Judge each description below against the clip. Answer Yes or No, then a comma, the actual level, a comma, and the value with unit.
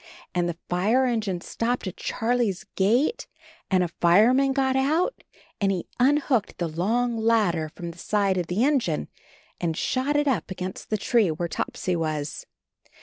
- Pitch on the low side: No, high, 205 Hz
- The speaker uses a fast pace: No, average, 165 wpm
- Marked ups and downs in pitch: Yes, wide, 6.1 semitones